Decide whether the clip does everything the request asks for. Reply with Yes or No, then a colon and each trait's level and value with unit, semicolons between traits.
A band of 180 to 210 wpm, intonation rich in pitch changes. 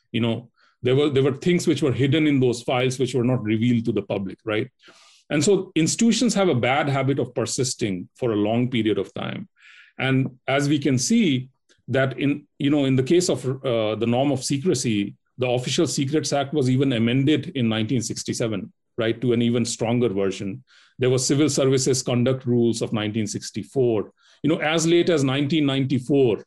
No: average, 190 wpm; average, 3.7 semitones